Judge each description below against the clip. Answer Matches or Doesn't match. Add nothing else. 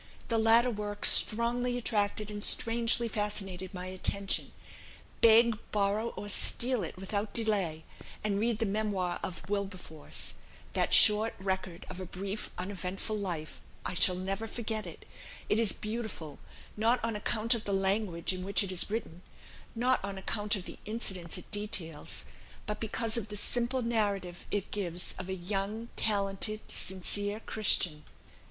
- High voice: Matches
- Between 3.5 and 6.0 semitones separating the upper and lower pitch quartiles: Doesn't match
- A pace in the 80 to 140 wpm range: Doesn't match